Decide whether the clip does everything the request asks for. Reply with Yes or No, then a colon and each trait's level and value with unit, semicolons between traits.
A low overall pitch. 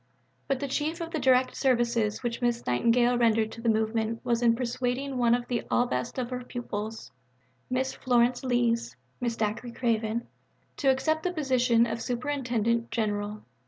No: high, 240 Hz